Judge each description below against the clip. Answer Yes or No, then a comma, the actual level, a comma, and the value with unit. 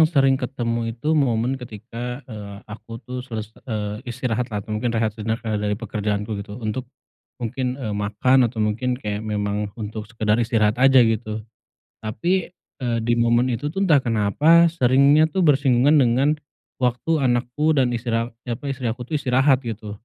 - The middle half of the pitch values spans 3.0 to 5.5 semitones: Yes, average, 3.4 semitones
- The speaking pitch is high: No, low, 120 Hz